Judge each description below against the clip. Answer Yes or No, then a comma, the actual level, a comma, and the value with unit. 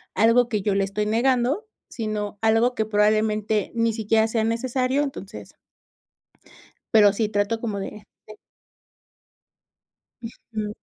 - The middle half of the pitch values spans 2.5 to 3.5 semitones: No, narrow, 1.8 semitones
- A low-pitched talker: No, high, 220 Hz